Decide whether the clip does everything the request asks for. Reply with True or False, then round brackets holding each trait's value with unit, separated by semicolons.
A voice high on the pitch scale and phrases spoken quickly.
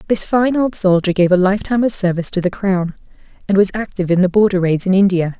True (195 Hz; 245 wpm)